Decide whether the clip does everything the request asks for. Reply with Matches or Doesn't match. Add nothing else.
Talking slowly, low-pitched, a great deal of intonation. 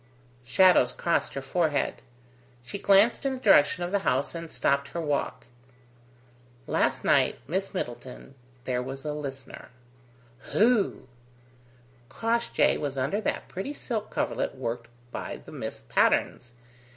Doesn't match